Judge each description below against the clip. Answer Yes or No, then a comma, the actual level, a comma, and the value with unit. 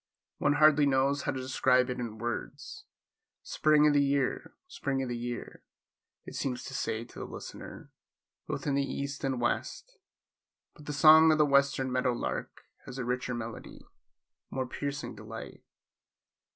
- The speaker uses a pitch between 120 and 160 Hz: Yes, low, 135 Hz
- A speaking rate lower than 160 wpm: No, average, 165 wpm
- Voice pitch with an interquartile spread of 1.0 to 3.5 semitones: Yes, narrow, 2.4 semitones